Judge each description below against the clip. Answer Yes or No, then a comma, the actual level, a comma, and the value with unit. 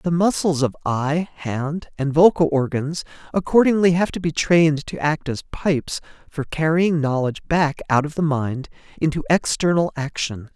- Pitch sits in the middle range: Yes, medium, 155 Hz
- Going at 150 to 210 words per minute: Yes, average, 160 wpm